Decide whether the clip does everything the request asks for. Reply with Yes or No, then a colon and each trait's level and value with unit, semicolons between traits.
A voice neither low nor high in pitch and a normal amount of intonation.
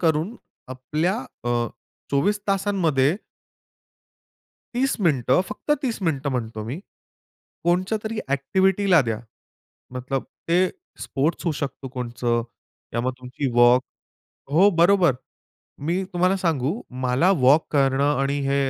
No: medium, 145 Hz; wide, 6.0 semitones